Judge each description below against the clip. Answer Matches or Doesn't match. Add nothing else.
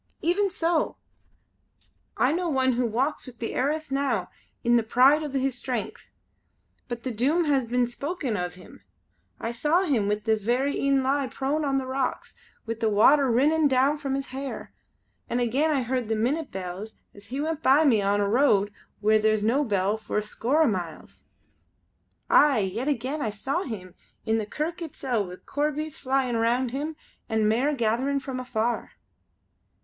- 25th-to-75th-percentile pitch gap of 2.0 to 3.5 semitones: Doesn't match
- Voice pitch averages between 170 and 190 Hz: Doesn't match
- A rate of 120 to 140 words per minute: Doesn't match